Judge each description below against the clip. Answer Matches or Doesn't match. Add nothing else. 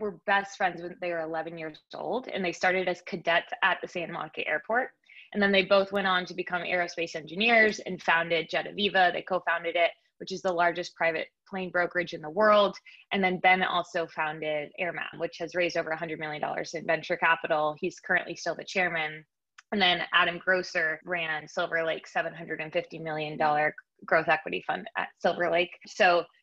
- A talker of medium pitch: Matches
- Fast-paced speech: Doesn't match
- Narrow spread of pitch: Matches